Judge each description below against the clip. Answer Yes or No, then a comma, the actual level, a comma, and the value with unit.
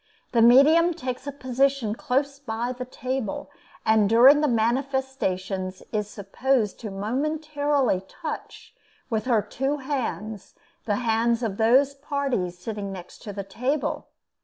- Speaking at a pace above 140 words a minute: No, slow, 135 wpm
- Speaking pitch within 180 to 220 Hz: No, high, 245 Hz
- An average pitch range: Yes, average, 4.5 semitones